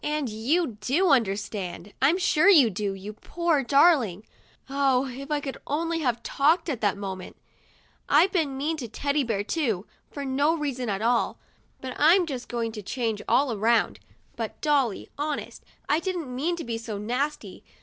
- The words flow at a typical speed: Yes, average, 185 wpm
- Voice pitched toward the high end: Yes, very high, 265 Hz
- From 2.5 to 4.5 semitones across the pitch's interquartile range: No, wide, 5.4 semitones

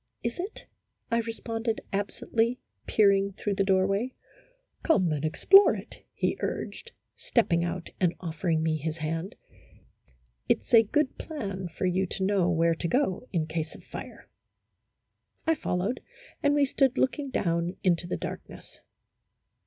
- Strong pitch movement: Yes, wide, 6.0 semitones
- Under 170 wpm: Yes, average, 160 wpm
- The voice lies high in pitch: Yes, high, 195 Hz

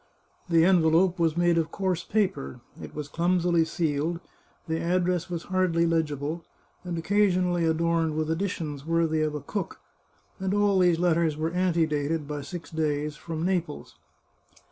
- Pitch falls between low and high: Yes, medium, 165 Hz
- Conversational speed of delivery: Yes, average, 155 wpm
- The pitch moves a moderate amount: No, narrow, 2.2 semitones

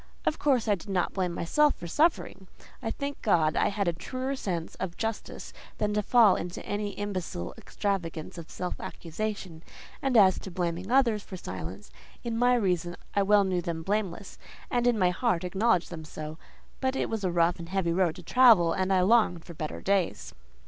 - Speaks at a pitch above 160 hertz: Yes, high, 190 Hz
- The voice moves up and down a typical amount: Yes, average, 4.3 semitones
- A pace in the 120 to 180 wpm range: No, average, 195 wpm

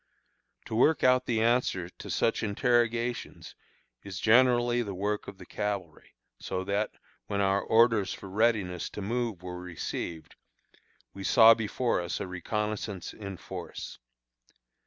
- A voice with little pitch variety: No, average, 3.6 semitones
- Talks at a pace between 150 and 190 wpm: No, slow, 135 wpm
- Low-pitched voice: Yes, low, 105 Hz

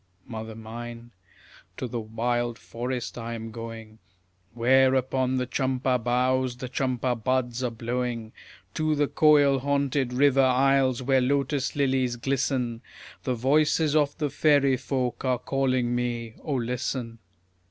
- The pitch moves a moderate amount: No, narrow, 2.2 semitones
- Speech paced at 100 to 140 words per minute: Yes, slow, 135 wpm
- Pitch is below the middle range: Yes, low, 125 Hz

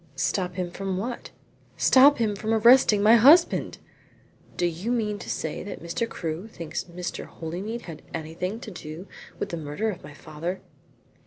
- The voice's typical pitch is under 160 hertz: No, high, 190 Hz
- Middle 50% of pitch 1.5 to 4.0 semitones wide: No, average, 4.8 semitones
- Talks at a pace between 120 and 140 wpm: No, average, 165 wpm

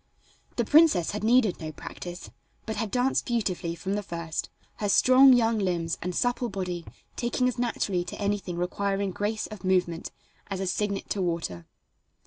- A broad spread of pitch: No, average, 4.2 semitones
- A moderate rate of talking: Yes, average, 165 wpm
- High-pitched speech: Yes, high, 200 Hz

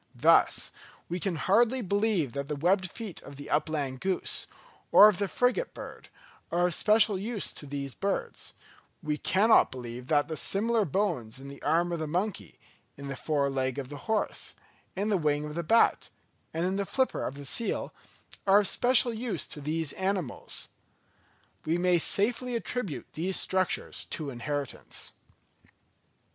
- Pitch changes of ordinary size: No, wide, 6.2 semitones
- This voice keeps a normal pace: Yes, average, 165 wpm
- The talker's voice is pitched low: No, medium, 175 Hz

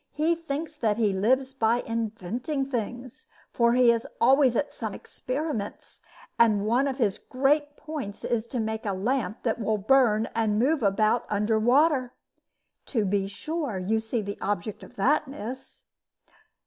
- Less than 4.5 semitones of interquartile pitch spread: Yes, average, 4.0 semitones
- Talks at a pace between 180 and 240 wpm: No, average, 160 wpm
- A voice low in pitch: No, high, 235 Hz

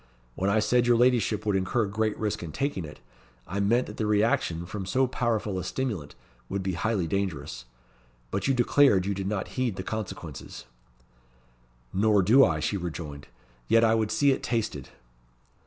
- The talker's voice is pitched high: No, low, 105 Hz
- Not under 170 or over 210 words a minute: Yes, average, 175 wpm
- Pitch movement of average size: Yes, average, 3.9 semitones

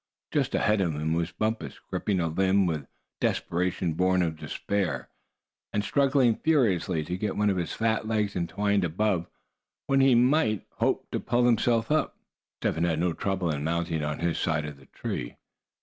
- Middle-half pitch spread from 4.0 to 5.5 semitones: Yes, average, 4.8 semitones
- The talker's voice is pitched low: Yes, very low, 95 Hz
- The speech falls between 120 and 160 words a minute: No, average, 180 wpm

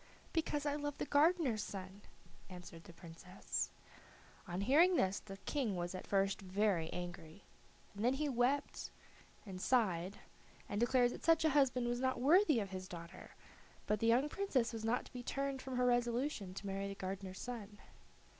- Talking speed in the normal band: Yes, average, 175 wpm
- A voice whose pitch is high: Yes, high, 225 Hz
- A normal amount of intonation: No, wide, 5.9 semitones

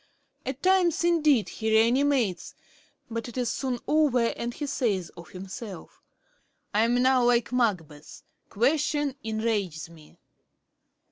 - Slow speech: Yes, slow, 130 wpm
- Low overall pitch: No, high, 240 Hz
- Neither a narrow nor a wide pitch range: Yes, average, 4.9 semitones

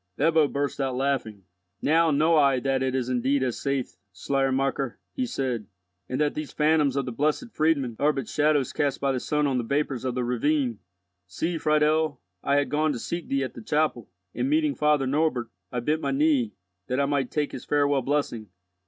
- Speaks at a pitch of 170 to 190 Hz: No, medium, 140 Hz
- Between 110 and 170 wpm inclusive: No, average, 200 wpm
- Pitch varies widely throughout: No, average, 2.8 semitones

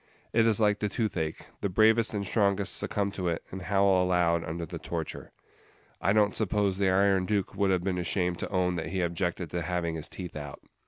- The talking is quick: Yes, fast, 210 wpm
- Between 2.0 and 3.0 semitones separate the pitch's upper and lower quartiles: Yes, narrow, 2.4 semitones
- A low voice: Yes, very low, 95 Hz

